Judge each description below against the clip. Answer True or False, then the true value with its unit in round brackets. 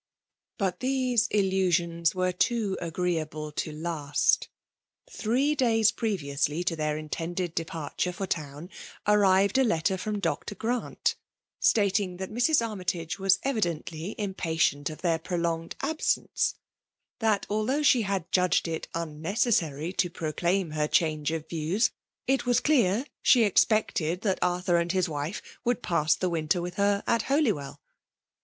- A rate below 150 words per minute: True (140 wpm)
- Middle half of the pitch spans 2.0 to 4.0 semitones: False (4.7 semitones)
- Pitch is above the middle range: False (180 Hz)